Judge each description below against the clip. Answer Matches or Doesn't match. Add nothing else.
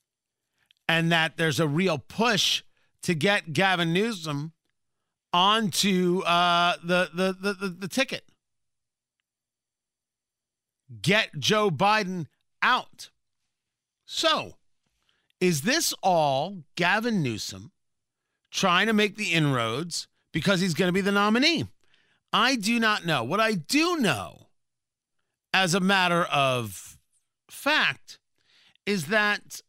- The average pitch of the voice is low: Doesn't match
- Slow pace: Matches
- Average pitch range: Matches